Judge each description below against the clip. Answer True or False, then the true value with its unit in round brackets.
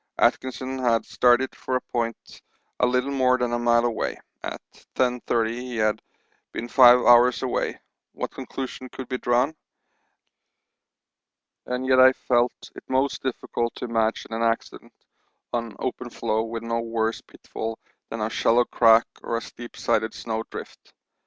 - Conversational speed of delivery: True (150 wpm)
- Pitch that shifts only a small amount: True (1.8 semitones)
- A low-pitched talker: True (120 Hz)